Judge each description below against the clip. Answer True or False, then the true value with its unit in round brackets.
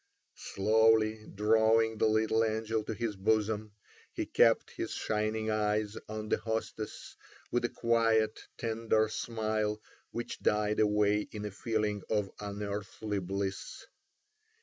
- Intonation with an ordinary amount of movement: False (1.0 semitones)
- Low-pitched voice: True (110 Hz)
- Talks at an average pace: False (125 wpm)